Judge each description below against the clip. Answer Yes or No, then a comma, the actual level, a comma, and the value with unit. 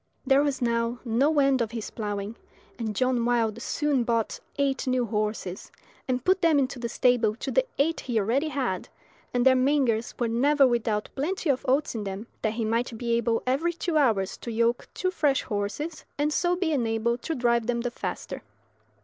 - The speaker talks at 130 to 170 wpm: No, average, 190 wpm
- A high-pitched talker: Yes, high, 245 Hz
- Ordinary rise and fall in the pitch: Yes, average, 3.7 semitones